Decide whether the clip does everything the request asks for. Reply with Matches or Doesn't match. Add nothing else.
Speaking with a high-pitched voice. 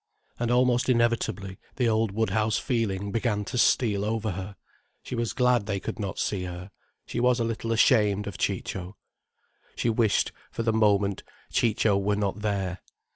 Doesn't match